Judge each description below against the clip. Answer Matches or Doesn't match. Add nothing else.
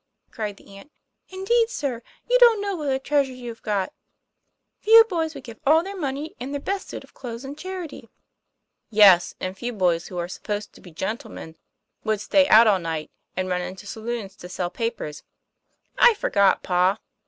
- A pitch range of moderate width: Doesn't match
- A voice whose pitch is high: Matches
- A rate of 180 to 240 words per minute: Matches